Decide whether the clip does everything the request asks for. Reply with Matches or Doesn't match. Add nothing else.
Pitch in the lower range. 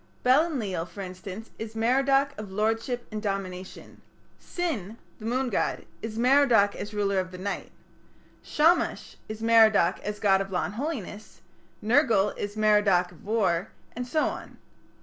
Doesn't match